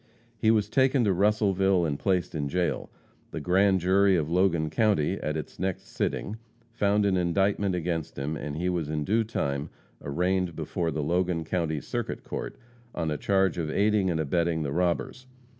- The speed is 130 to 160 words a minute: No, average, 175 wpm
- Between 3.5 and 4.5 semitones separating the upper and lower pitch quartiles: Yes, average, 3.8 semitones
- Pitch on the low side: Yes, very low, 90 Hz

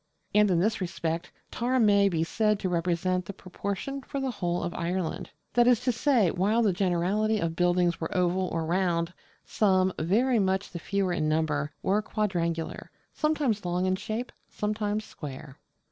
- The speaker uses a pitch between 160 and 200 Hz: Yes, medium, 185 Hz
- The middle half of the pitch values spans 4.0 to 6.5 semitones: No, average, 3.6 semitones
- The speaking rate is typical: Yes, average, 170 wpm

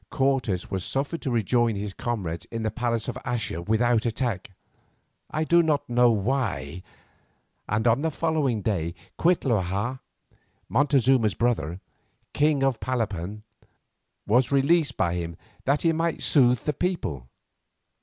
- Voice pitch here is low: Yes, low, 120 Hz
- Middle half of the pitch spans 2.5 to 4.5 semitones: No, average, 5.2 semitones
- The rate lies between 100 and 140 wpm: Yes, slow, 135 wpm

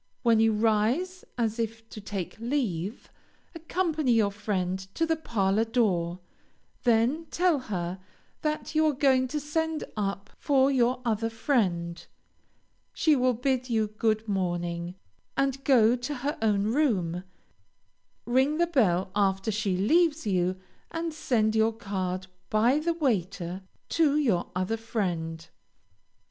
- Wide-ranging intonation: Yes, wide, 6.0 semitones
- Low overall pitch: No, high, 225 Hz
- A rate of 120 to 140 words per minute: Yes, slow, 135 wpm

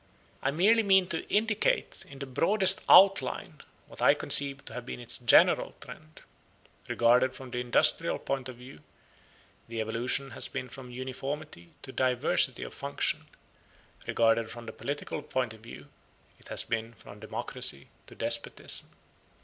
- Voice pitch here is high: No, low, 130 Hz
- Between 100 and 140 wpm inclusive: No, average, 150 wpm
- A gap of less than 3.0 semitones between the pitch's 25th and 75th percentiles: No, average, 3.6 semitones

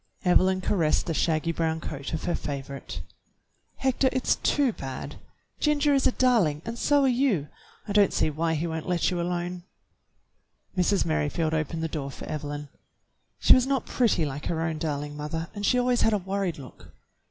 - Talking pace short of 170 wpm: No, average, 185 wpm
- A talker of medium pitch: Yes, medium, 170 Hz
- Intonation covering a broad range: Yes, wide, 5.8 semitones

